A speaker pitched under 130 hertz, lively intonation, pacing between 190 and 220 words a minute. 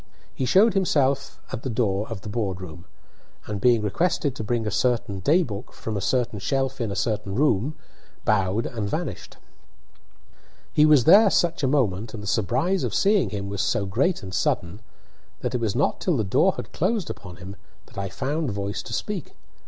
Yes: low, 115 Hz; wide, 5.9 semitones; average, 200 wpm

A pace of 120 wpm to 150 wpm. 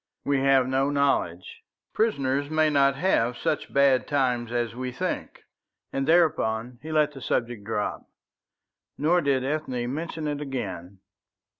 Yes: average, 140 wpm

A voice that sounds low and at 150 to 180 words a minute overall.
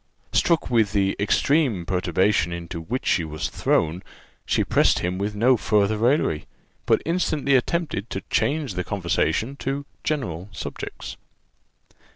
No: low, 105 Hz; slow, 135 wpm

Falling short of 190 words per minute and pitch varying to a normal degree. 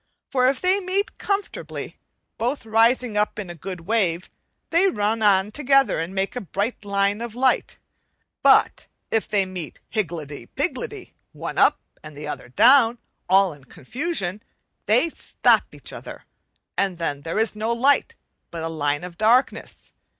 No: average, 155 wpm; wide, 6.0 semitones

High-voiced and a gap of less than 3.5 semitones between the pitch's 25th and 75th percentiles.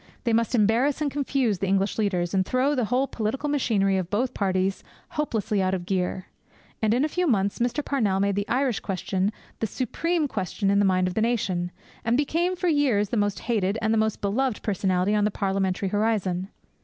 No: high, 210 Hz; average, 4.7 semitones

